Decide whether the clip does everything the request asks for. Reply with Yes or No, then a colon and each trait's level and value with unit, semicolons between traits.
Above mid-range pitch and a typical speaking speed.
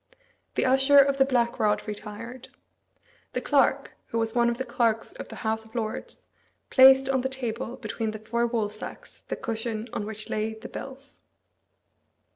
Yes: high, 235 Hz; average, 170 wpm